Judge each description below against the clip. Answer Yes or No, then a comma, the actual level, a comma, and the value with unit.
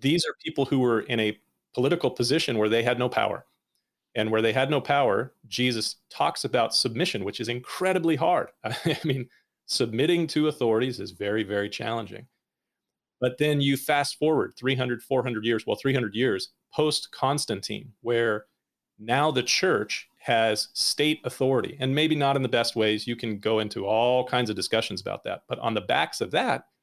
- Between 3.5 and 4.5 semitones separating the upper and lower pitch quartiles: Yes, average, 3.9 semitones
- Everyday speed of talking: Yes, average, 180 wpm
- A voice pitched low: Yes, low, 125 Hz